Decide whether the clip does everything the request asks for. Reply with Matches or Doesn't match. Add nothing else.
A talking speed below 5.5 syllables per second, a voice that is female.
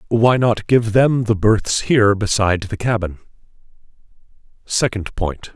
Doesn't match